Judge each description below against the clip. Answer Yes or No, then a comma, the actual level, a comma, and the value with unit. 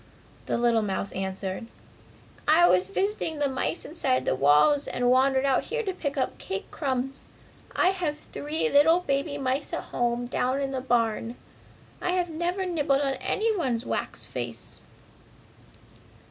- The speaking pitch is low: No, very high, 275 Hz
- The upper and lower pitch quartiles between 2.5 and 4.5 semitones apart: No, average, 5.1 semitones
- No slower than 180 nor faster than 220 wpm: No, average, 150 wpm